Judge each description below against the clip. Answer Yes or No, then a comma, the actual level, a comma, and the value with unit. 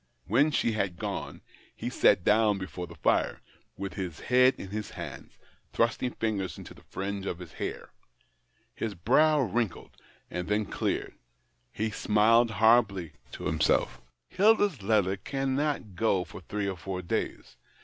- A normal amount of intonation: Yes, average, 4.0 semitones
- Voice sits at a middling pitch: No, low, 105 Hz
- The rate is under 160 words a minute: Yes, average, 150 wpm